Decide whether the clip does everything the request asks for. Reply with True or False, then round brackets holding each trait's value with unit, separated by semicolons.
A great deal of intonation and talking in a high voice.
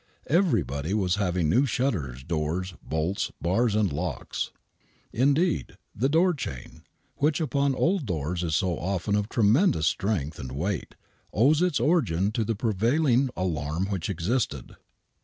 False (8.2 semitones; 100 Hz)